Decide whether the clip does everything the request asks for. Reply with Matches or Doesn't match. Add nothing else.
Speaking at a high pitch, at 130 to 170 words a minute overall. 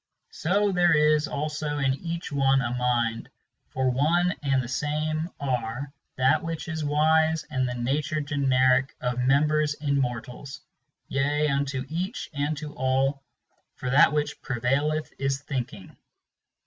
Doesn't match